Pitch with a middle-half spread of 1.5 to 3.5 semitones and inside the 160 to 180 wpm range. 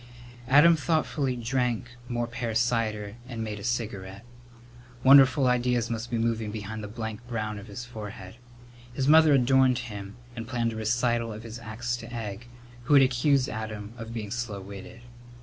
Yes: narrow, 2.4 semitones; average, 165 wpm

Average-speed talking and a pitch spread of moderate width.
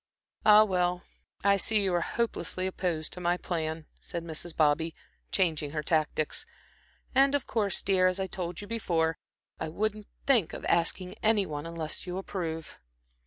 Yes: average, 165 wpm; average, 3.7 semitones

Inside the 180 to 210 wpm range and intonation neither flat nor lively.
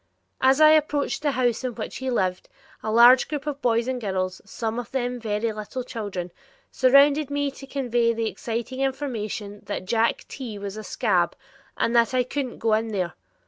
Yes: average, 185 wpm; average, 3.6 semitones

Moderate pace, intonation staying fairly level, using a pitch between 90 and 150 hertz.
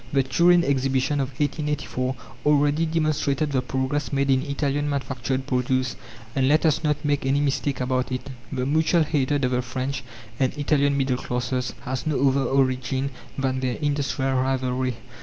Yes: average, 160 wpm; narrow, 2.1 semitones; low, 135 Hz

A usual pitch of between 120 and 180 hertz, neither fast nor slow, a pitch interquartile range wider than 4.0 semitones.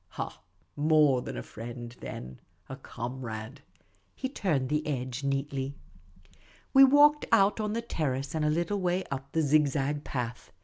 Yes: medium, 140 Hz; average, 165 wpm; average, 4.5 semitones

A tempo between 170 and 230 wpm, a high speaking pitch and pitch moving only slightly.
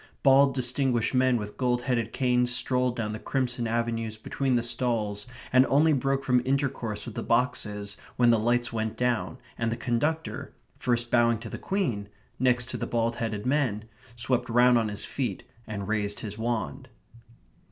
No: average, 175 wpm; low, 120 Hz; narrow, 2.3 semitones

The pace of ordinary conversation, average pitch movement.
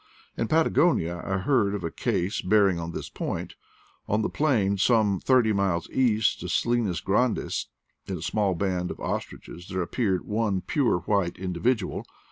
Yes: average, 160 wpm; average, 3.9 semitones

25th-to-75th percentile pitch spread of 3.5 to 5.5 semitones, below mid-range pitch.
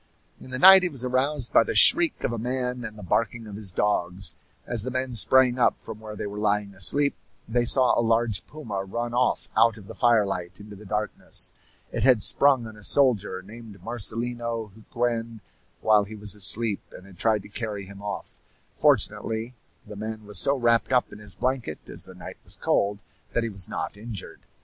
No: average, 3.0 semitones; low, 110 Hz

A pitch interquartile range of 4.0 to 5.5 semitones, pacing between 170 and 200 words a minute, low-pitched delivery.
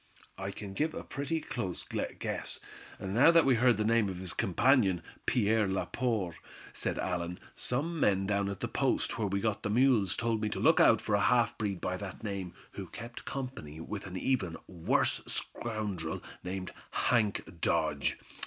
Yes: average, 4.3 semitones; average, 175 wpm; low, 105 Hz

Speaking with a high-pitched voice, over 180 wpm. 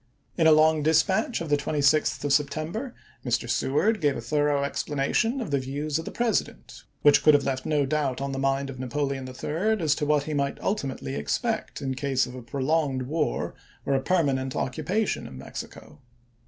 No: medium, 145 Hz; average, 195 wpm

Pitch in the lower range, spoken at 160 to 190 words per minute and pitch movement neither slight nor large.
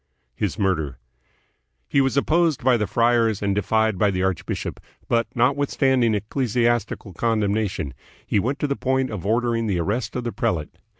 Yes: low, 115 Hz; average, 165 wpm; average, 3.9 semitones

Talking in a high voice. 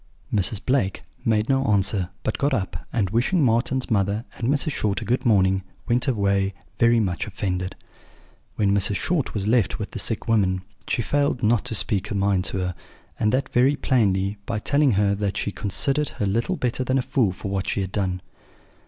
No: low, 105 Hz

